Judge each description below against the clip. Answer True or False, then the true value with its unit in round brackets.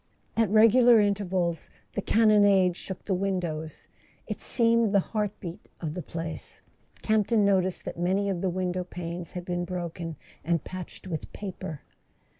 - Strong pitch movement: False (2.8 semitones)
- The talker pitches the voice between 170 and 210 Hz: True (185 Hz)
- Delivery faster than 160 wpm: False (155 wpm)